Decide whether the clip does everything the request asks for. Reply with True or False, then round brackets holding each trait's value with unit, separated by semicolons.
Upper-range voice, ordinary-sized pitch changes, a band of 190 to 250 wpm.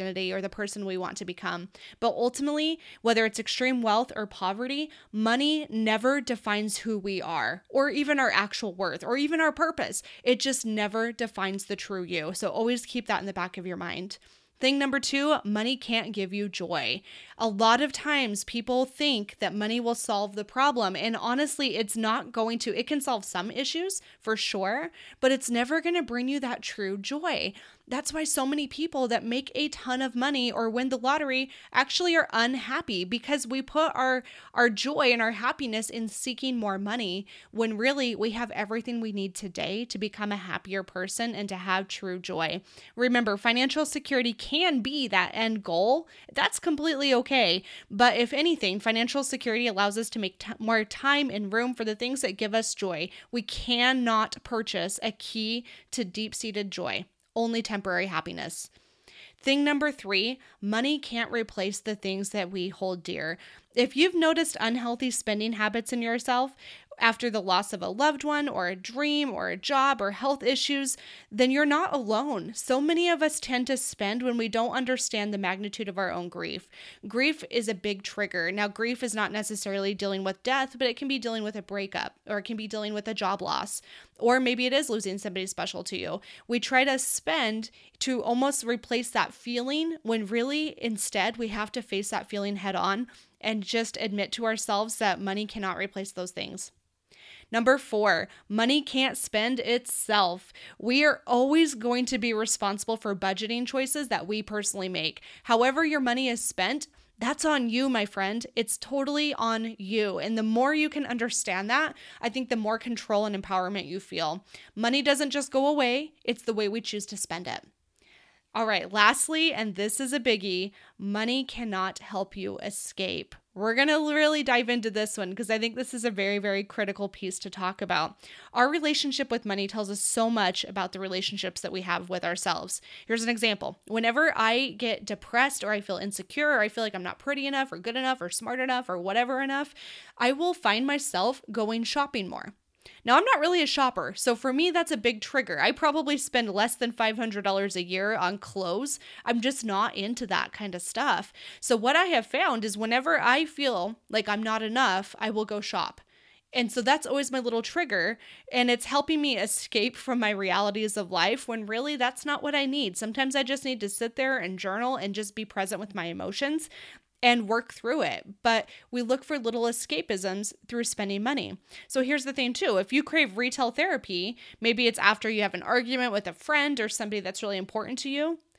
True (230 Hz; 4.3 semitones; 195 wpm)